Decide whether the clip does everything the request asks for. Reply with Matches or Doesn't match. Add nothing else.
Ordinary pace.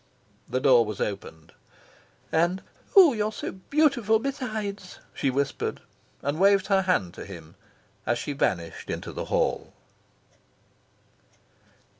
Doesn't match